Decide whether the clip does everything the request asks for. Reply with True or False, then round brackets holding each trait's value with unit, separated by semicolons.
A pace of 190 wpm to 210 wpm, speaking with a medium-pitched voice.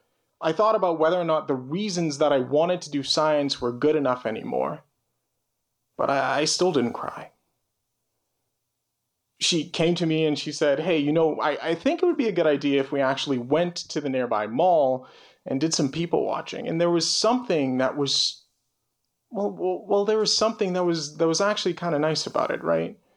True (205 wpm; 155 Hz)